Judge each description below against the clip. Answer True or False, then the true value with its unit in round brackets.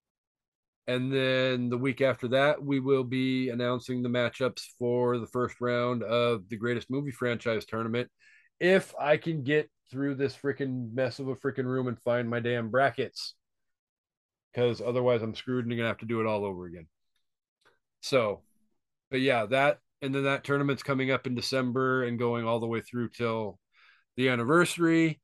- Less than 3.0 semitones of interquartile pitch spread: True (2.4 semitones)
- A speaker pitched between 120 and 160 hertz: True (125 Hz)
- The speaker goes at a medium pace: True (175 wpm)